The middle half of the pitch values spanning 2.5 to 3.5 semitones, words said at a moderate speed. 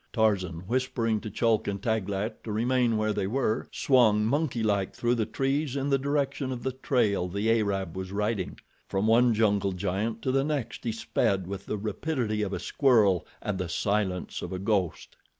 No: average, 3.9 semitones; average, 185 wpm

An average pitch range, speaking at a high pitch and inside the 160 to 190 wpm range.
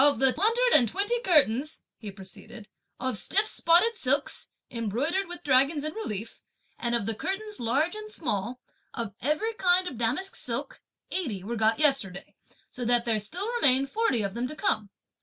No: wide, 7.9 semitones; very high, 270 Hz; average, 175 wpm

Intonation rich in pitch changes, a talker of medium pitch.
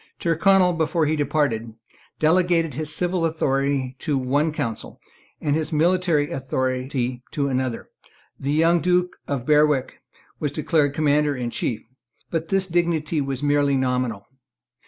No: average, 3.6 semitones; medium, 150 Hz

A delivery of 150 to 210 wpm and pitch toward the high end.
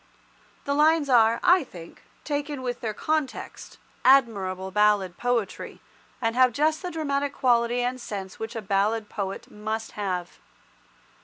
No: average, 140 wpm; high, 235 Hz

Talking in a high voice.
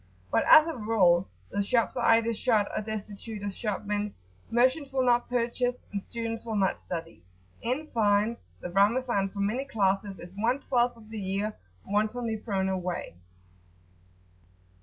Yes: high, 215 Hz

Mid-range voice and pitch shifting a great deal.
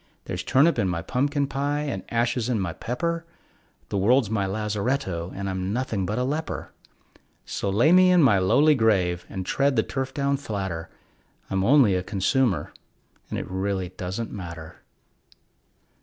No: low, 110 Hz; wide, 6.5 semitones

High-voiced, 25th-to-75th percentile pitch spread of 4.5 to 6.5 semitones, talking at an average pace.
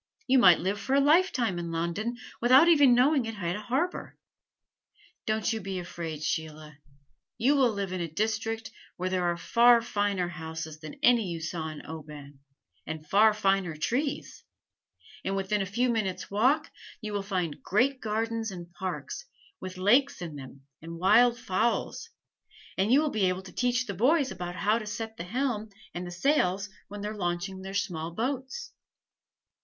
Yes: high, 200 Hz; wide, 5.4 semitones; average, 175 wpm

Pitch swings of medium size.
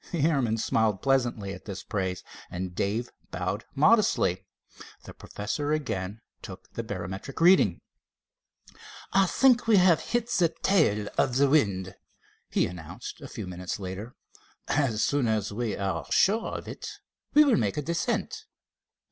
No: wide, 9.0 semitones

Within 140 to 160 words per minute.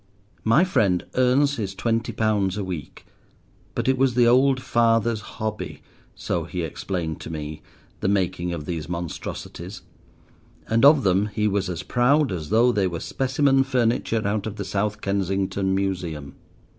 Yes: average, 155 wpm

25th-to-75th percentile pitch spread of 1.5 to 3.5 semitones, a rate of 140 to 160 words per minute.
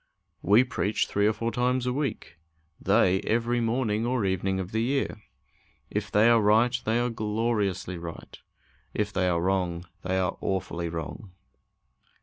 No: average, 3.9 semitones; average, 155 wpm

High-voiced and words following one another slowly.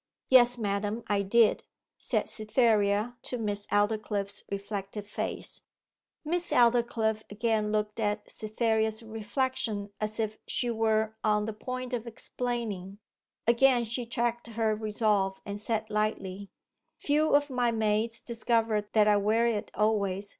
Yes: high, 220 Hz; slow, 130 wpm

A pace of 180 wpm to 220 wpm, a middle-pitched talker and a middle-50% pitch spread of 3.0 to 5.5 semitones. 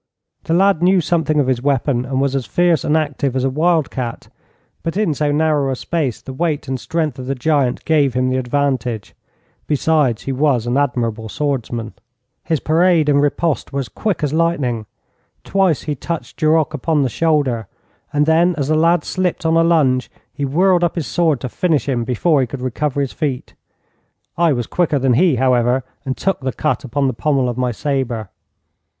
Yes: average, 195 wpm; medium, 145 Hz; average, 4.0 semitones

